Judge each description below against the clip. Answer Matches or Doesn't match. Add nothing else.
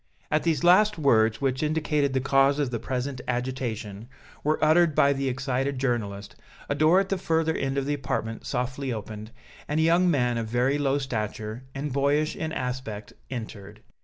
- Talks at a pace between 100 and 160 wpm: Doesn't match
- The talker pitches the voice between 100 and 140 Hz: Matches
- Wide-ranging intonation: Doesn't match